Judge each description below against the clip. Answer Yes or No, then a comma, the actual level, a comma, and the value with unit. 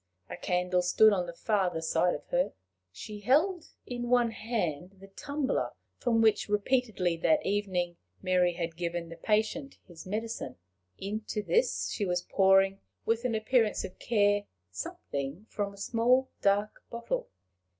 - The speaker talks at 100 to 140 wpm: No, average, 150 wpm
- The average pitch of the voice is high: Yes, high, 205 Hz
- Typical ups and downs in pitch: Yes, average, 4.3 semitones